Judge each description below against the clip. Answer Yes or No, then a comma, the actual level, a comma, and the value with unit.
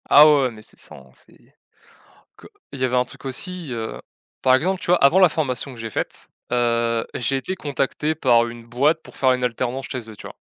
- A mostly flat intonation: No, average, 4.0 semitones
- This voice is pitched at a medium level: No, low, 130 Hz